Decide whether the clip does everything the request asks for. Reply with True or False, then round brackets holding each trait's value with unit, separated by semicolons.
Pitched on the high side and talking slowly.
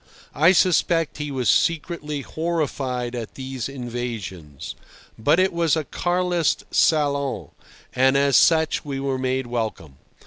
False (140 Hz; 130 wpm)